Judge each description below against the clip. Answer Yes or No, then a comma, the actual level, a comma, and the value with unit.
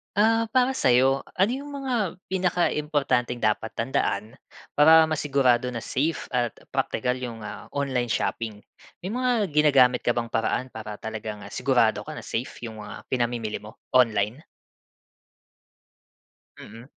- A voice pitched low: Yes, low, 125 Hz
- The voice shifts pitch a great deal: Yes, wide, 6.0 semitones